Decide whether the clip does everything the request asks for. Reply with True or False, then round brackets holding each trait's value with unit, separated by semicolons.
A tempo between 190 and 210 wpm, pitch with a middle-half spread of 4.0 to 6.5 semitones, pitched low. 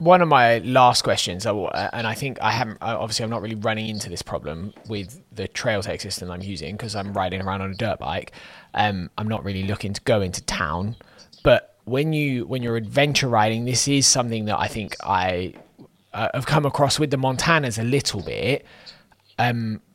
True (200 wpm; 4.3 semitones; 110 Hz)